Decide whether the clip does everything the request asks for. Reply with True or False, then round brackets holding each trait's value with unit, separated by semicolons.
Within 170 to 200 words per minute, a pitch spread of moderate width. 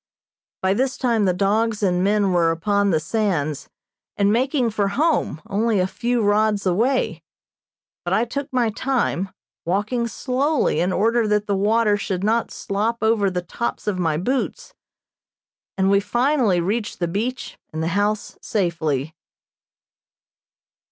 False (145 wpm; 3.9 semitones)